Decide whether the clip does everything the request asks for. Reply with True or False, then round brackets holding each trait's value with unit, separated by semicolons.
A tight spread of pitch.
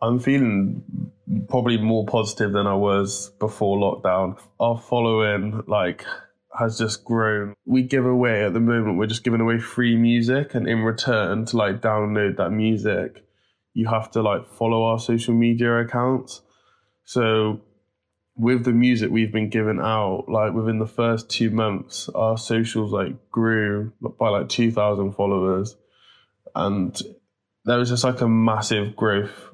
True (2.2 semitones)